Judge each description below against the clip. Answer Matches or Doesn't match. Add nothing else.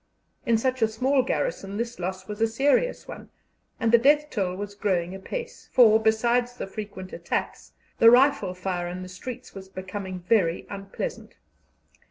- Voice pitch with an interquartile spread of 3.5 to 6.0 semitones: Matches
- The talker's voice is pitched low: Doesn't match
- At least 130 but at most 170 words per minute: Matches